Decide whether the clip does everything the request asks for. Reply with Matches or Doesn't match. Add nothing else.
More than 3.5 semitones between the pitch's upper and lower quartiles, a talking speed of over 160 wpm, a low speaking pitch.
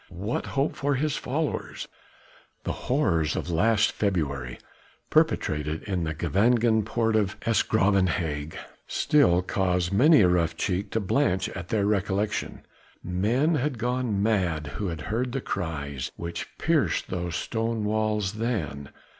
Doesn't match